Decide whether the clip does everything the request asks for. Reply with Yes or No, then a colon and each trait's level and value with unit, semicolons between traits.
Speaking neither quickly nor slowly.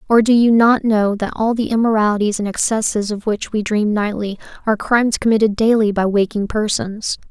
Yes: average, 190 wpm